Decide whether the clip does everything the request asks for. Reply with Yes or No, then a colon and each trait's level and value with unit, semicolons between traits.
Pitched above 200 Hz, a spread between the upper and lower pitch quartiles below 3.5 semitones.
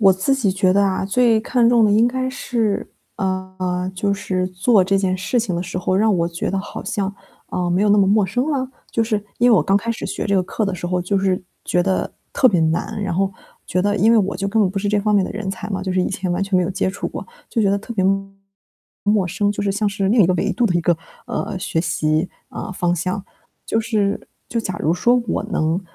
No: high, 195 Hz; narrow, 2.6 semitones